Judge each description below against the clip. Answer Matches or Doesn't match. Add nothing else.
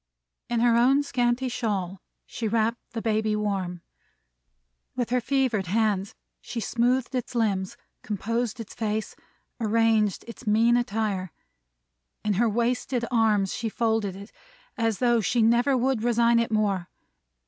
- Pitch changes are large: Doesn't match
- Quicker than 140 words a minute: Doesn't match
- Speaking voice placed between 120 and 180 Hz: Doesn't match